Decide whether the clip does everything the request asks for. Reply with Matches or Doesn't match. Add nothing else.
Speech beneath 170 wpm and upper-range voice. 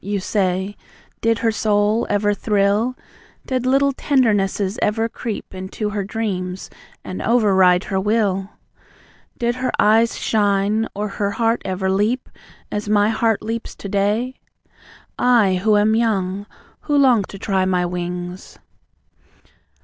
Matches